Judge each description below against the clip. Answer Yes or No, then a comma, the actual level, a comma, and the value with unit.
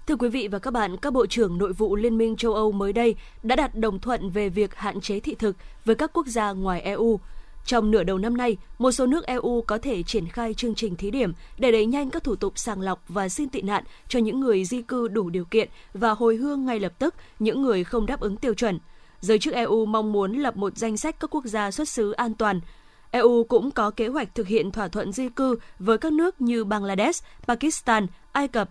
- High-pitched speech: Yes, high, 225 Hz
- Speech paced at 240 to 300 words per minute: Yes, average, 245 wpm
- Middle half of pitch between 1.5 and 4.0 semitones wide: Yes, average, 3.1 semitones